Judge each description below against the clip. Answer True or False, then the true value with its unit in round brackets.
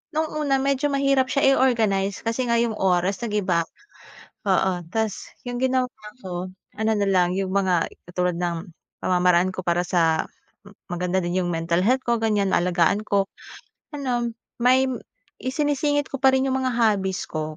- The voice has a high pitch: True (200 Hz)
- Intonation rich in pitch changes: True (6.2 semitones)